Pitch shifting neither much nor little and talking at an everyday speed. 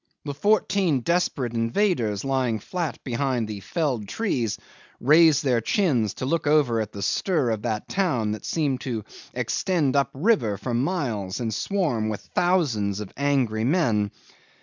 No: wide, 6.7 semitones; average, 150 wpm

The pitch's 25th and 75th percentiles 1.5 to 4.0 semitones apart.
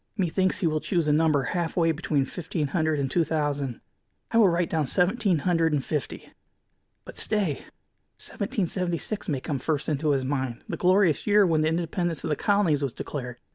Yes: average, 3.6 semitones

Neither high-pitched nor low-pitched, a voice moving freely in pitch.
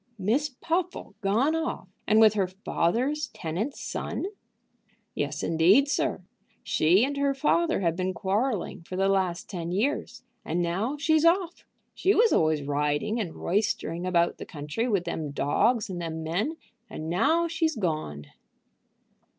No: high, 200 Hz; wide, 8.7 semitones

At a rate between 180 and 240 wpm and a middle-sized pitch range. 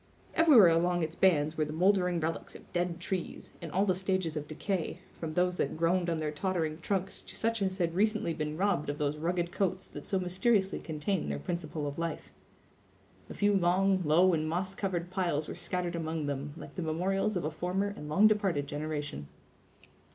Yes: average, 195 wpm; average, 3.4 semitones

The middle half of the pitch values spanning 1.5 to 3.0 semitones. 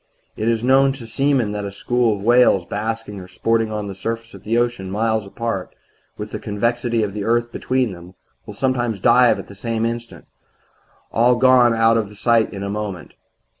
Yes: narrow, 2.6 semitones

